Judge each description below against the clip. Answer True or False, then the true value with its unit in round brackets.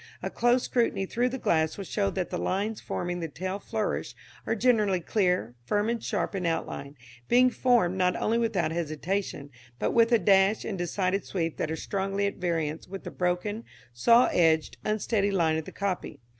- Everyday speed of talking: True (185 wpm)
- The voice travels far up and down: False (4.1 semitones)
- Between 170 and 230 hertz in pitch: True (190 Hz)